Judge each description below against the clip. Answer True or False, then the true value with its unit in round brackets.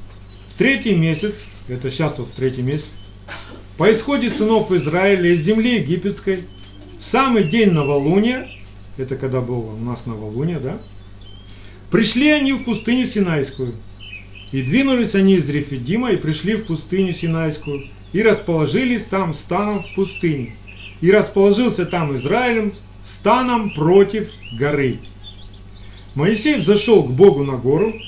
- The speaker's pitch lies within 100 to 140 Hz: False (160 Hz)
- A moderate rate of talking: True (125 wpm)